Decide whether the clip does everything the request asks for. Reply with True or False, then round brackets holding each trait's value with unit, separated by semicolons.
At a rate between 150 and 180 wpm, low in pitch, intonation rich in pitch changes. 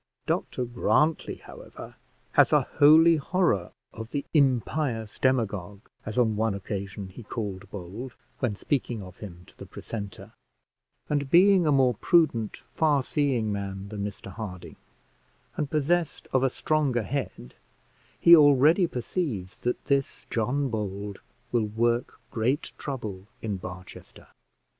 False (135 wpm; 120 Hz; 5.9 semitones)